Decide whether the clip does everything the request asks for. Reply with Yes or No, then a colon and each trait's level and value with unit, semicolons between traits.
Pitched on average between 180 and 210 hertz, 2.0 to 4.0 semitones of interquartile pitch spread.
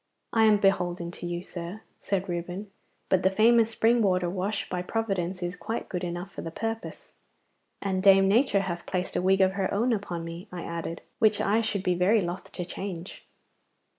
Yes: high, 190 Hz; average, 3.0 semitones